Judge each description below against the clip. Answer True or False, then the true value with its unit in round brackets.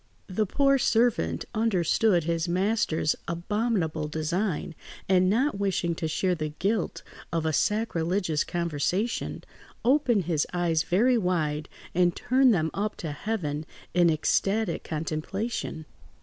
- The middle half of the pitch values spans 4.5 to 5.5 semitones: True (5.1 semitones)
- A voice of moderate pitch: True (180 Hz)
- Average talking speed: False (120 wpm)